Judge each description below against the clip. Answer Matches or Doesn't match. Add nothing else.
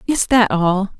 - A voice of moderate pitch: Doesn't match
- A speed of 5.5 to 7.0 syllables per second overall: Doesn't match